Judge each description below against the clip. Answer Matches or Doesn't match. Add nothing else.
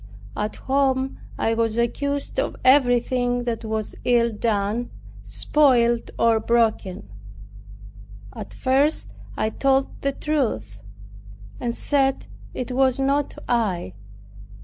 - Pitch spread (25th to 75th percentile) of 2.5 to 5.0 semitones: Matches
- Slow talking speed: Matches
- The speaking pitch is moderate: Doesn't match